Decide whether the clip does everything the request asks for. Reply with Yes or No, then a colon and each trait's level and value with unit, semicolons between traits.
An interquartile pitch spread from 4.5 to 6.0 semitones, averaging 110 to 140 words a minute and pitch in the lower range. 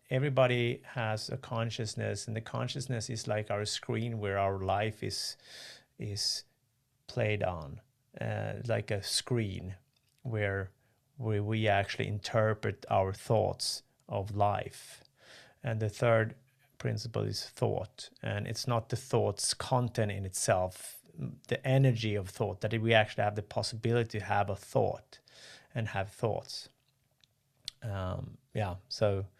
No: average, 3.3 semitones; slow, 135 wpm; low, 110 Hz